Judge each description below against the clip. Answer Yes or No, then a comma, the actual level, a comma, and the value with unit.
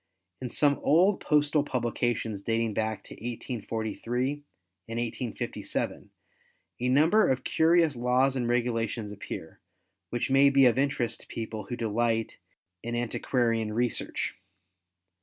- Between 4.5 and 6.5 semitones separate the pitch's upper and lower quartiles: No, average, 3.1 semitones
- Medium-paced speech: No, slow, 120 wpm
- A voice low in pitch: Yes, low, 120 Hz